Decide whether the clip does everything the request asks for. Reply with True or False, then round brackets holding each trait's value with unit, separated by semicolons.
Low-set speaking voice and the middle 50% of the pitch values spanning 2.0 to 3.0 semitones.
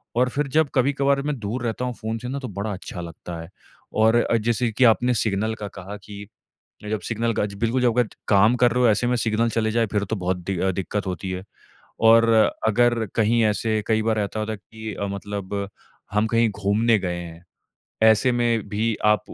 True (110 Hz; 2.7 semitones)